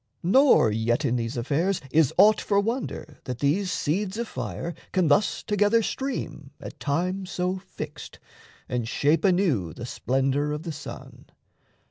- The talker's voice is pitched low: No, medium, 165 Hz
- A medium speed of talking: Yes, average, 150 wpm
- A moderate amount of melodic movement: No, wide, 6.3 semitones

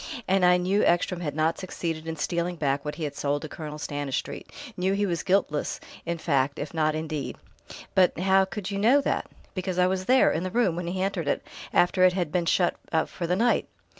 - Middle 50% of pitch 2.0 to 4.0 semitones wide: Yes, average, 3.1 semitones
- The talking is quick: Yes, fast, 225 wpm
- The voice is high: No, medium, 175 Hz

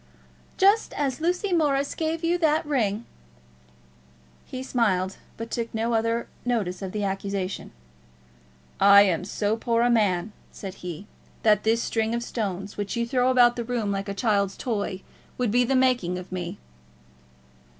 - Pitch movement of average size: Yes, average, 4.0 semitones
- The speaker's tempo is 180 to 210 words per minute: No, average, 160 wpm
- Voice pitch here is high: Yes, high, 225 Hz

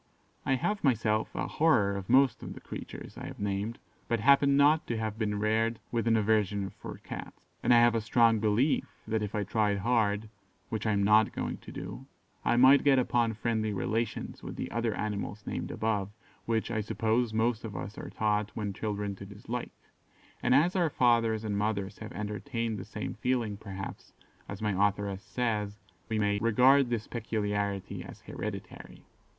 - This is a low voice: Yes, low, 110 Hz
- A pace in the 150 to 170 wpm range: No, average, 185 wpm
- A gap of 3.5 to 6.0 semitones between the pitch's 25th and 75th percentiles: No, narrow, 2.4 semitones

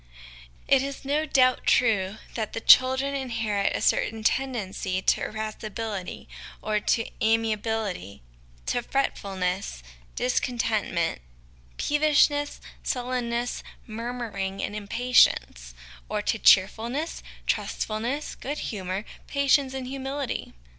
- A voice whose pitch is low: No, high, 230 Hz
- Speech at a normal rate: No, slow, 105 wpm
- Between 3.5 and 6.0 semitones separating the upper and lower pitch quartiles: Yes, average, 4.2 semitones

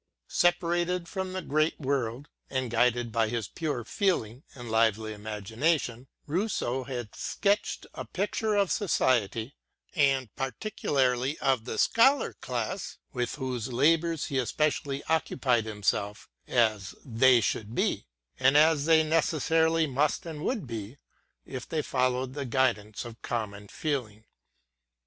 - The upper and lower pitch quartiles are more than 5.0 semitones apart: Yes, wide, 5.5 semitones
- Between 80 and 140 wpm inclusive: Yes, slow, 135 wpm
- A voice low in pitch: Yes, low, 130 Hz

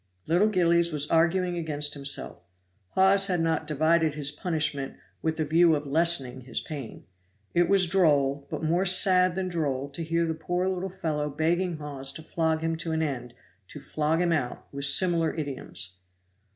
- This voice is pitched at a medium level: Yes, medium, 160 Hz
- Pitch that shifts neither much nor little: Yes, average, 3.0 semitones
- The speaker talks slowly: No, average, 175 wpm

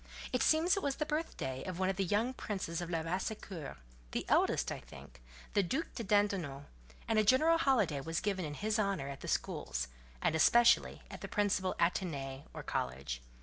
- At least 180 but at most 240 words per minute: Yes, average, 185 wpm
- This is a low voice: No, high, 190 Hz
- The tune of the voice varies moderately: No, wide, 7.4 semitones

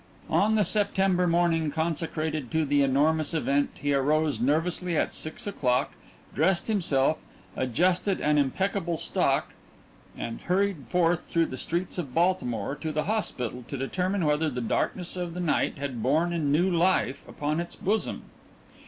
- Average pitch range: Yes, average, 4.1 semitones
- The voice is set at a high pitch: No, medium, 160 Hz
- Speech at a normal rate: Yes, average, 155 wpm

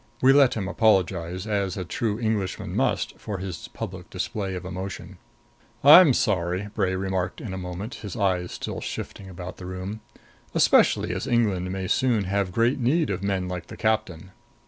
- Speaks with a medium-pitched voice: No, very low, 95 Hz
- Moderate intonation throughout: Yes, average, 3.0 semitones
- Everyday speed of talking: Yes, average, 170 wpm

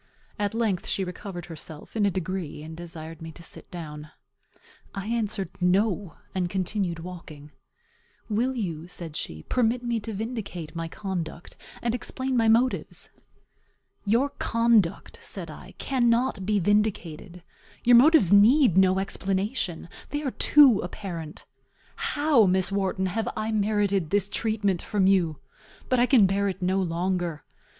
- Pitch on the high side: Yes, high, 195 Hz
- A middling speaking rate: Yes, average, 145 wpm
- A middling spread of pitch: Yes, average, 4.3 semitones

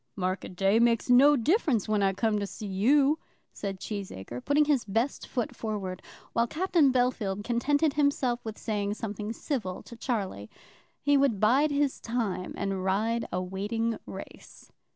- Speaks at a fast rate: No, average, 155 wpm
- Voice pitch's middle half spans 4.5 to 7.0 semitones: Yes, average, 5.2 semitones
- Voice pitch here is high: Yes, high, 225 Hz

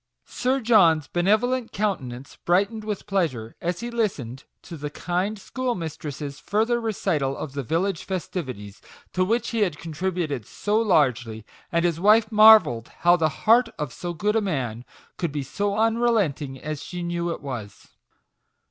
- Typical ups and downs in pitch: No, wide, 6.8 semitones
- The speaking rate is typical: Yes, average, 160 wpm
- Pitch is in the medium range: Yes, medium, 175 Hz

